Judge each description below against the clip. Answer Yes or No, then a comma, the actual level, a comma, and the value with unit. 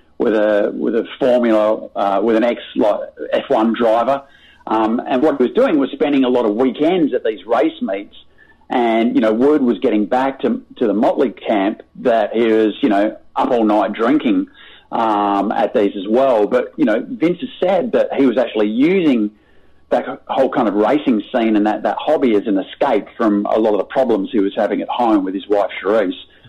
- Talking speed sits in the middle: No, fast, 210 wpm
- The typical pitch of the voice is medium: No, low, 125 Hz